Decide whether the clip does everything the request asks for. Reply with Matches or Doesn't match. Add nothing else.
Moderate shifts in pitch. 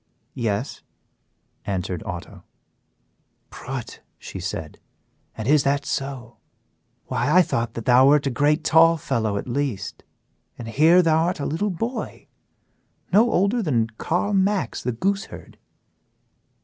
Doesn't match